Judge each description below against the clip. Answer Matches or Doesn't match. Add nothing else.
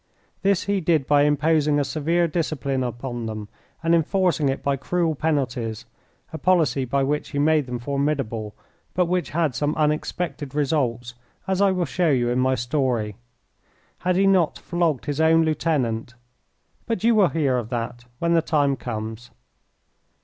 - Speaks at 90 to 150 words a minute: Doesn't match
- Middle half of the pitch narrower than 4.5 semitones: Doesn't match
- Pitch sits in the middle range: Matches